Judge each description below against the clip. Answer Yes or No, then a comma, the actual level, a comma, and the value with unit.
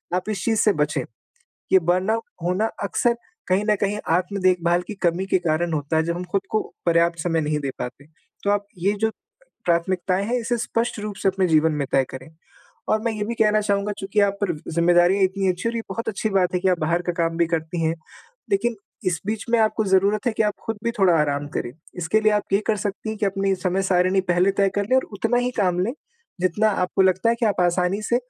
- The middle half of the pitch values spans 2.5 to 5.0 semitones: Yes, average, 3.5 semitones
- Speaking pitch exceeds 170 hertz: Yes, high, 190 Hz